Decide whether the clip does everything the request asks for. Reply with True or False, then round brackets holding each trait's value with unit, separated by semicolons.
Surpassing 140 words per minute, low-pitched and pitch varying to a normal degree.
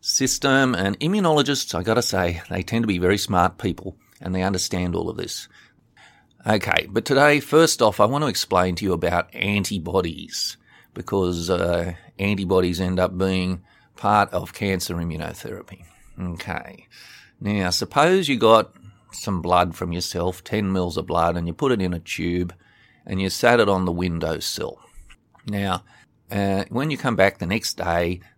True (165 wpm; 95 Hz; 4.1 semitones)